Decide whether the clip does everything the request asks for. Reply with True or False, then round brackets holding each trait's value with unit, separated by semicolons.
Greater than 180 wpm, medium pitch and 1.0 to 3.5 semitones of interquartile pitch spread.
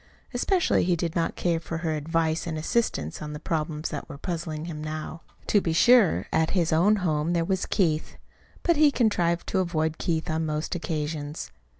True (190 wpm; 165 Hz; 2.4 semitones)